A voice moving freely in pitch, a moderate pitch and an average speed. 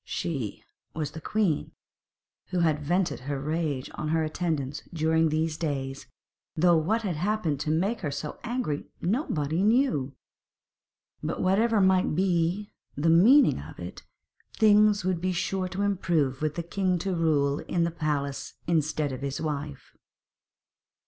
No: average, 4.2 semitones; medium, 165 Hz; average, 150 wpm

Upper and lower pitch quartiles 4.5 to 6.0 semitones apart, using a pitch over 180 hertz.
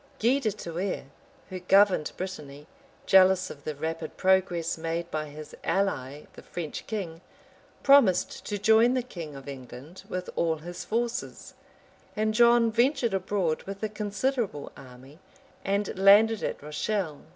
Yes: average, 5.3 semitones; high, 190 Hz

